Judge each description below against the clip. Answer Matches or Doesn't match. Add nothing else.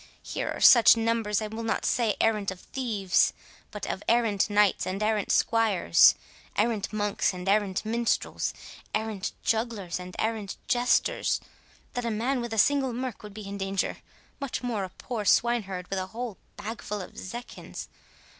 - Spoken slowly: Doesn't match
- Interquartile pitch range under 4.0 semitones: Matches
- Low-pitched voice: Doesn't match